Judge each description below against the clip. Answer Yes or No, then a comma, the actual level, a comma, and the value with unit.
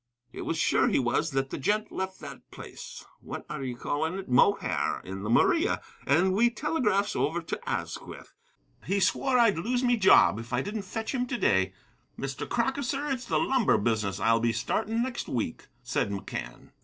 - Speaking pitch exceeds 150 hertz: Yes, high, 190 Hz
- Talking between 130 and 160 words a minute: No, average, 190 wpm